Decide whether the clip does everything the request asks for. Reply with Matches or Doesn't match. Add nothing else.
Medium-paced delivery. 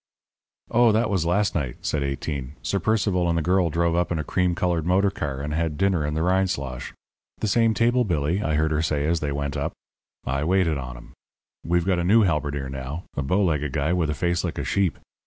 Doesn't match